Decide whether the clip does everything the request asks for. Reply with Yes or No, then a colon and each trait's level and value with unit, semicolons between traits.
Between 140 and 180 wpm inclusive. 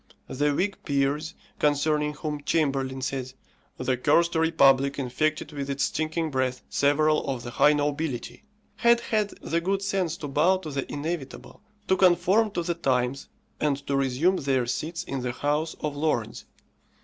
Yes: average, 160 wpm